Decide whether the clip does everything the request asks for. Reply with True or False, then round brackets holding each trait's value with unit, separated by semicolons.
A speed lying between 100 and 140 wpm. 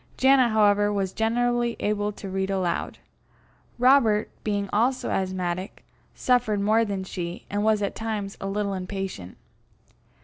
True (135 wpm)